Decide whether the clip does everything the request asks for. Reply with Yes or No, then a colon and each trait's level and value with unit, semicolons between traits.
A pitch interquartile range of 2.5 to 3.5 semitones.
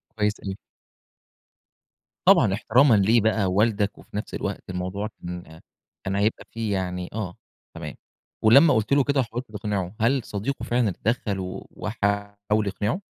Yes: average, 2.8 semitones